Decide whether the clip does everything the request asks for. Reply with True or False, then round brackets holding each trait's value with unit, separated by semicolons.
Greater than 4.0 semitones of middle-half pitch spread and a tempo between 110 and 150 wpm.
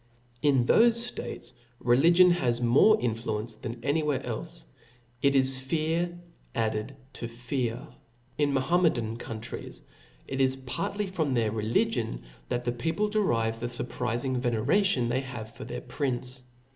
True (4.5 semitones; 145 wpm)